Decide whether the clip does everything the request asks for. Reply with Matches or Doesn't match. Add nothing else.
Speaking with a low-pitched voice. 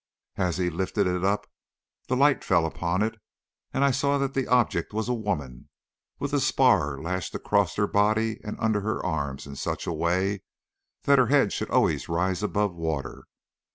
Matches